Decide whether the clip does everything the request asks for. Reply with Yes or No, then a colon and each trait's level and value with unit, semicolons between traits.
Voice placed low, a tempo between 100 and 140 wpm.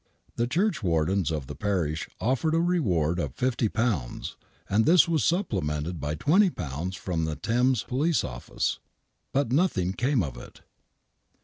Yes: low, 105 Hz; slow, 135 wpm